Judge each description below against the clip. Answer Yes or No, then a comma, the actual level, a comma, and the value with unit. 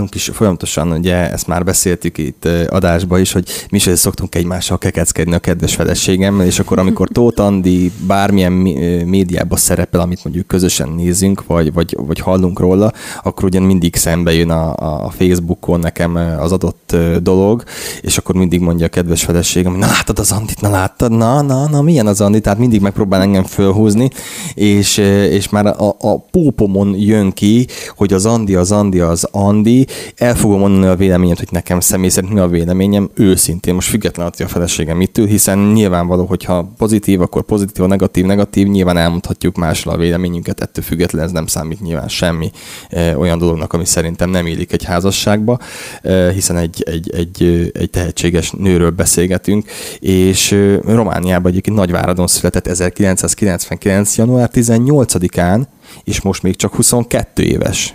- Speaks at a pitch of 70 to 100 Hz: Yes, very low, 95 Hz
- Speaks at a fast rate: Yes, fast, 165 wpm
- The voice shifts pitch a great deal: No, average, 2.7 semitones